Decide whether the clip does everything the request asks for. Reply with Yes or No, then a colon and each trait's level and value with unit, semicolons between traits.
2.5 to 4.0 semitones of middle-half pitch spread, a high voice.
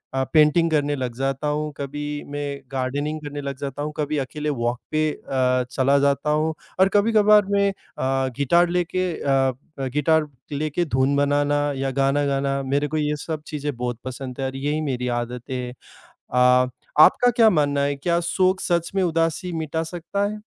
No: average, 3.0 semitones; medium, 145 Hz